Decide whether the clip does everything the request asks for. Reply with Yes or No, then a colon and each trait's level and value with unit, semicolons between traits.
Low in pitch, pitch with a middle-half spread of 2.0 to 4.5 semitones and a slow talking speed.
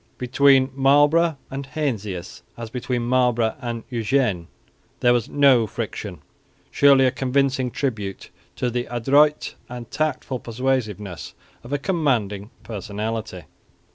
Yes: low, 125 Hz; average, 3.6 semitones; slow, 115 wpm